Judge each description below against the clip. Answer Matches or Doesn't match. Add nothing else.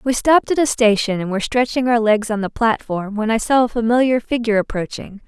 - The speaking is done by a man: Doesn't match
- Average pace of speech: Doesn't match